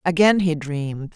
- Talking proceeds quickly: No, average, 155 wpm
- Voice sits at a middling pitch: Yes, medium, 165 Hz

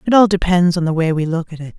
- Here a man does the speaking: No, female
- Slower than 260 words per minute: No, fast, 335 wpm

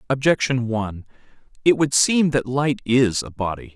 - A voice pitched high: No, low, 125 Hz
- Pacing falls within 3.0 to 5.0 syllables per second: Yes, 4.8 syllables/s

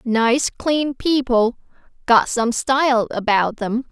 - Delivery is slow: Yes, slow, 125 wpm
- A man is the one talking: No, female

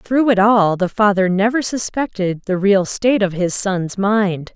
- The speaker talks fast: No, average, 185 wpm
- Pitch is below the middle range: No, high, 200 Hz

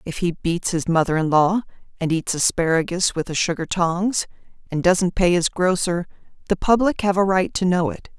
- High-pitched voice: No, medium, 175 Hz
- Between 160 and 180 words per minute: No, average, 200 wpm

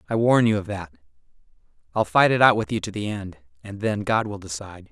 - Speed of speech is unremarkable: No, fast, 230 wpm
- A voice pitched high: No, low, 100 Hz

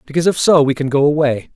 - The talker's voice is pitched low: No, medium, 145 Hz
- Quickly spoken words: Yes, fast, 270 wpm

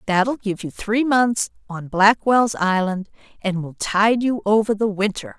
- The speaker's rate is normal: Yes, average, 165 wpm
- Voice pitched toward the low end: No, high, 205 Hz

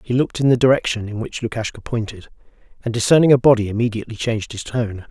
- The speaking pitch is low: Yes, low, 115 Hz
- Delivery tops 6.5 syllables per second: Yes, 7.0 syllables/s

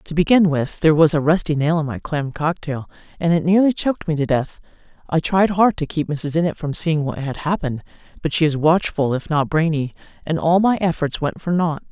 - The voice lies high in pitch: No, medium, 160 Hz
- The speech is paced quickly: Yes, fast, 225 wpm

